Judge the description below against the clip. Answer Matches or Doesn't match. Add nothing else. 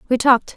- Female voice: Matches